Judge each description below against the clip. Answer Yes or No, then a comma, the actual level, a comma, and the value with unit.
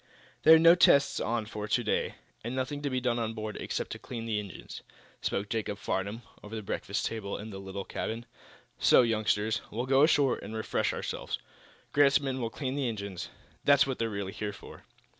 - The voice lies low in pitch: Yes, low, 115 Hz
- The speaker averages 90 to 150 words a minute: No, average, 200 wpm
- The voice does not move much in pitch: No, average, 3.8 semitones